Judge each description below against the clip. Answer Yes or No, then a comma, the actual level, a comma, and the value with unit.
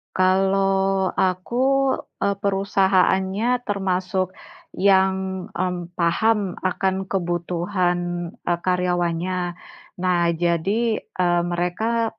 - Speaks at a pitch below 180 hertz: No, medium, 185 Hz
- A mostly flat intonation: Yes, narrow, 1.8 semitones